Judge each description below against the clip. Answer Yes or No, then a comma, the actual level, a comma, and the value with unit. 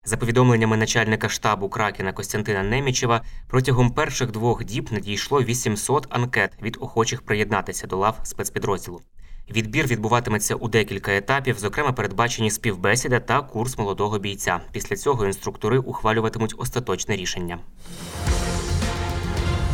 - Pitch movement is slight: No, average, 3.4 semitones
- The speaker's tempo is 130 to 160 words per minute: No, average, 115 wpm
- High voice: No, low, 110 Hz